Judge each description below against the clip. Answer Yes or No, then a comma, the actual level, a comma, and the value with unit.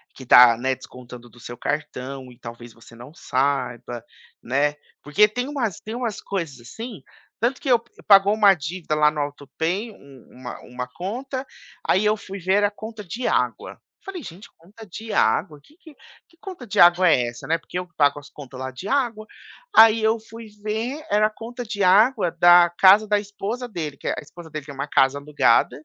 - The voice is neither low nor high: Yes, medium, 175 Hz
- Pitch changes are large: Yes, wide, 7.8 semitones